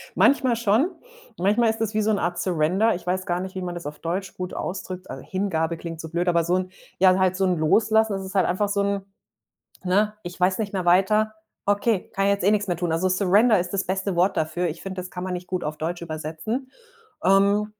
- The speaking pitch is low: No, medium, 185 Hz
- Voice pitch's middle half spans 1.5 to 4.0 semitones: Yes, narrow, 2.5 semitones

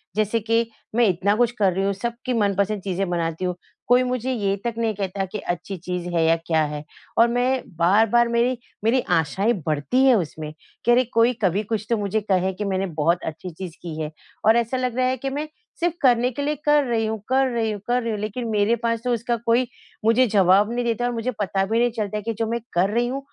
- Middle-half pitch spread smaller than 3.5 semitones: No, average, 4.0 semitones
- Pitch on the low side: No, high, 220 Hz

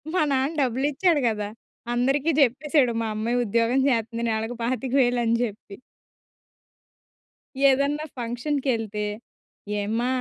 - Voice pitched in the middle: No, high, 245 Hz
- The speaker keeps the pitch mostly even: No, average, 3.1 semitones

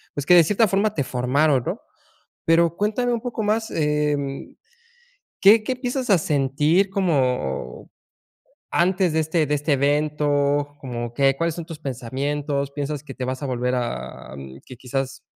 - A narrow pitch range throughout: No, average, 4.4 semitones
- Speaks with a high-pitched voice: No, medium, 145 Hz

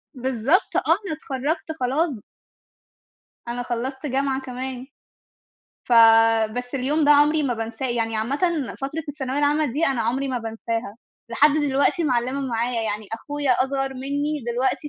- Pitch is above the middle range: Yes, very high, 265 Hz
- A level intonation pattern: No, average, 3.5 semitones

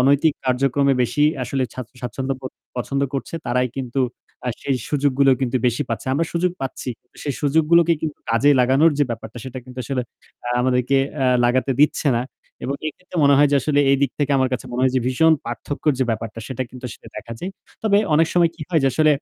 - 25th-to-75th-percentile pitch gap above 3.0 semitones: No, average, 2.7 semitones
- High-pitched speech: No, low, 135 Hz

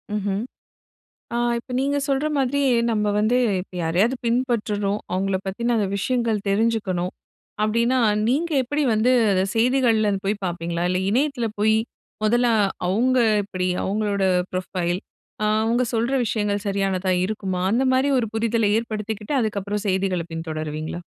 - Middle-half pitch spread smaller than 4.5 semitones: Yes, average, 3.5 semitones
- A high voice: Yes, high, 210 Hz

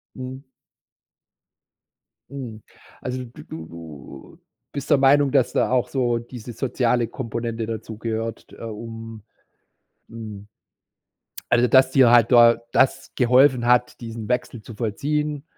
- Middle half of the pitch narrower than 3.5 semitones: Yes, narrow, 2.5 semitones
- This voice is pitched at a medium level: No, low, 120 Hz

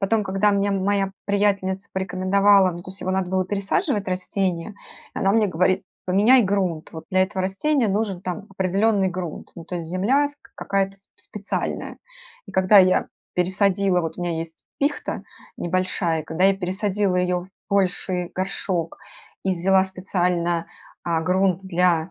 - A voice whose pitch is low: No, high, 190 Hz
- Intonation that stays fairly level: Yes, narrow, 1.7 semitones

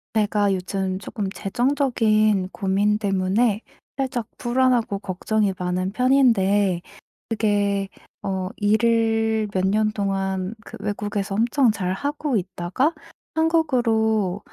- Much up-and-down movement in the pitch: No, average, 3.1 semitones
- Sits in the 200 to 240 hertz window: Yes, high, 210 Hz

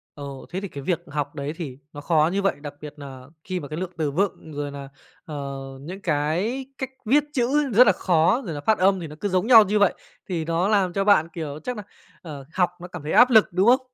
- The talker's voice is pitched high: No, medium, 175 Hz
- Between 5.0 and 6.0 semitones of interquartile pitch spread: Yes, wide, 5.6 semitones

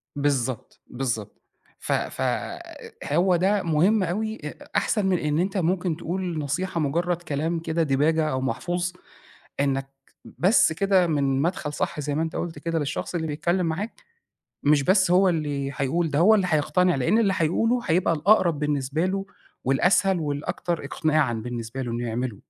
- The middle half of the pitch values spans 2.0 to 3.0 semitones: No, average, 4.3 semitones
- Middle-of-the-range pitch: Yes, medium, 160 Hz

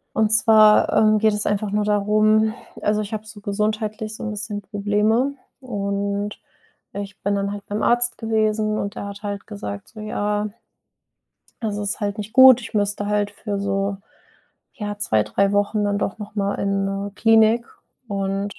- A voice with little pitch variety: Yes, narrow, 1.2 semitones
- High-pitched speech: Yes, high, 210 Hz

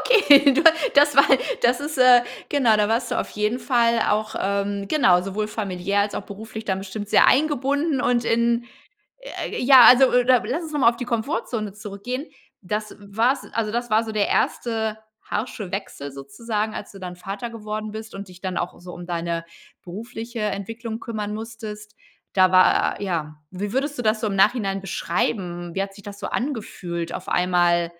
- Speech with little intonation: No, average, 3.6 semitones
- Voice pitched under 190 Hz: No, high, 215 Hz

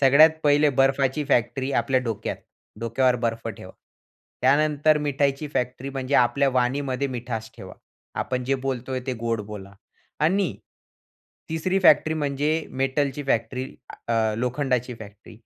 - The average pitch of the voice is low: Yes, low, 130 Hz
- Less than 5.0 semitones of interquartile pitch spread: Yes, average, 2.8 semitones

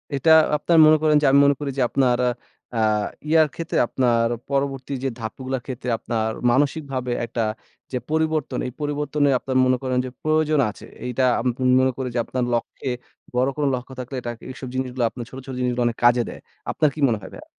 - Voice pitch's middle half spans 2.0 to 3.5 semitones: Yes, average, 2.8 semitones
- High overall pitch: No, low, 130 Hz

